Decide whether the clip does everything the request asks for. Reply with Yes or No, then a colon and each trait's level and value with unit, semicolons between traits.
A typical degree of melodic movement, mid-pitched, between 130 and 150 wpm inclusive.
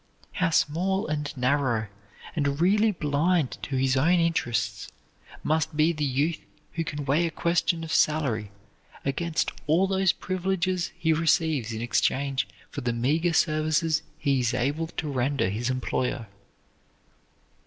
Yes: average, 4.1 semitones; medium, 150 Hz; average, 140 wpm